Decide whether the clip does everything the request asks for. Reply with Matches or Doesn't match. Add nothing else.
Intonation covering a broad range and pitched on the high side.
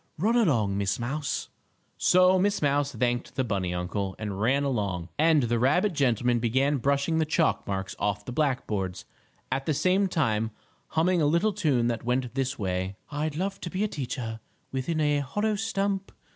Doesn't match